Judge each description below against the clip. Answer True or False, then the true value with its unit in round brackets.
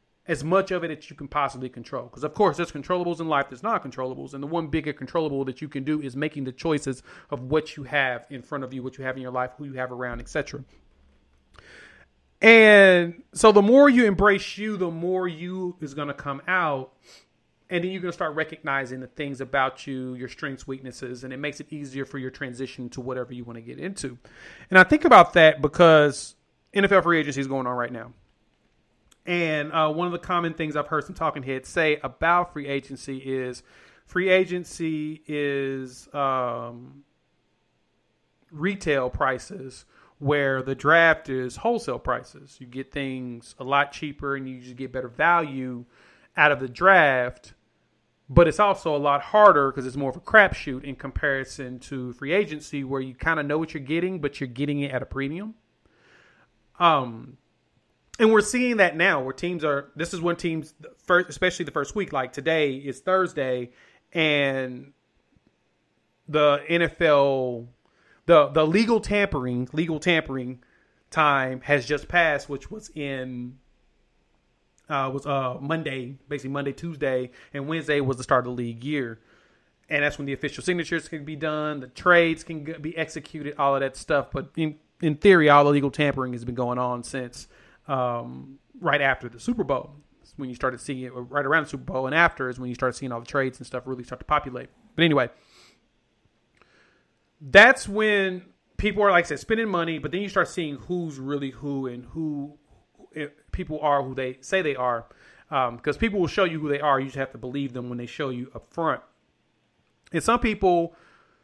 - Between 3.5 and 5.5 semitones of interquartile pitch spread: True (4.2 semitones)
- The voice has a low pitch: False (145 Hz)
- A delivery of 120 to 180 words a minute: False (190 wpm)